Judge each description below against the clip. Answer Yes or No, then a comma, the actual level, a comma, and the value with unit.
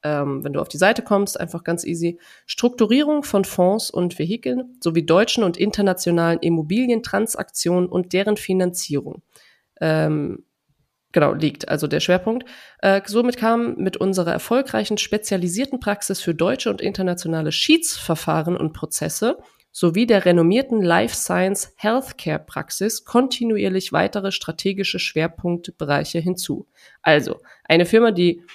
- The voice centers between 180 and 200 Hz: Yes, medium, 185 Hz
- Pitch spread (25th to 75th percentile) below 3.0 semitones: No, average, 4.1 semitones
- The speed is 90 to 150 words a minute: Yes, slow, 125 wpm